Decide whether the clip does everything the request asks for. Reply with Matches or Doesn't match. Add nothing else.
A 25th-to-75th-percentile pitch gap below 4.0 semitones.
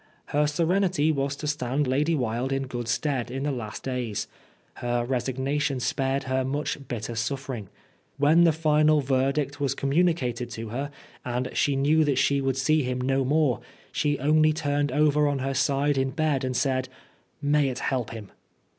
Matches